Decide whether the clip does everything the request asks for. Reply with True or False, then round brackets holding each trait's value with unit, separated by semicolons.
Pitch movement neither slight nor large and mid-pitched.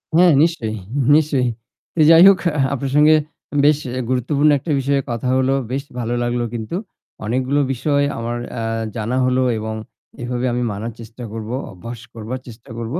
False (3.5 semitones; 125 Hz)